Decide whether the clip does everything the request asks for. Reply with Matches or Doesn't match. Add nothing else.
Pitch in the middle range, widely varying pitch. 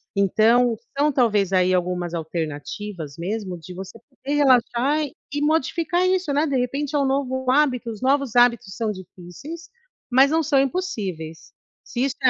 Doesn't match